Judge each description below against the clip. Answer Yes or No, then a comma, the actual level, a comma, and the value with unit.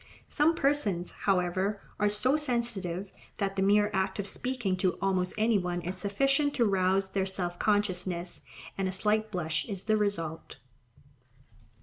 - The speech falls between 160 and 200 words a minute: No, average, 150 wpm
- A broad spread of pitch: No, average, 2.7 semitones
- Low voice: No, high, 195 Hz